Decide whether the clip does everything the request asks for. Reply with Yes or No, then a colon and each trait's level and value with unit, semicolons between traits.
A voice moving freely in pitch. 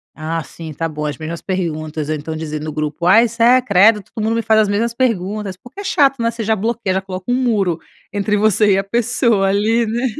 Yes: wide, 5.7 semitones